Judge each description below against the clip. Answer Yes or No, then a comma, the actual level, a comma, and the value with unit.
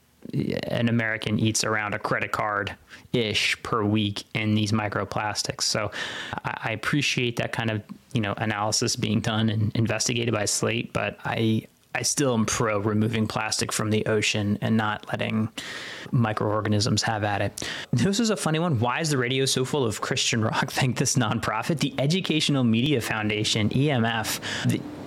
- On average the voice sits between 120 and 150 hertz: No, low, 110 Hz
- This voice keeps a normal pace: Yes, average, 165 wpm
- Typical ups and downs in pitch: Yes, average, 3.1 semitones